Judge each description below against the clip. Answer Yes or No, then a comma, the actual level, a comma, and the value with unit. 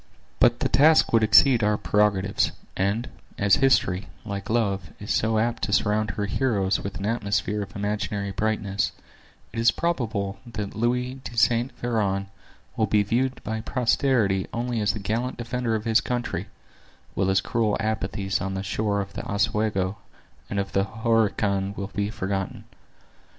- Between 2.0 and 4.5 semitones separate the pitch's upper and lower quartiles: Yes, average, 2.8 semitones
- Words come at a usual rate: Yes, average, 160 wpm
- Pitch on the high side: No, low, 105 Hz